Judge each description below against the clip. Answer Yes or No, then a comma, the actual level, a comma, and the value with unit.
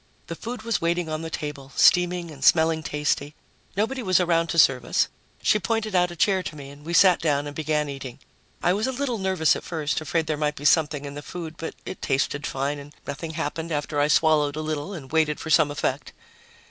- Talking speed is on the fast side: Yes, fast, 225 wpm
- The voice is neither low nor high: Yes, medium, 160 Hz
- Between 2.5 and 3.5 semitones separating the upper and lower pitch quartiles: Yes, average, 3.2 semitones